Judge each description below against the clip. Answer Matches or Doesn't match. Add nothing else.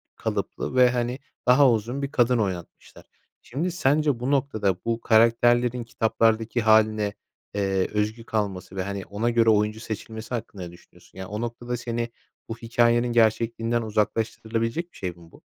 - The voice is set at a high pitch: Doesn't match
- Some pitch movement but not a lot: Doesn't match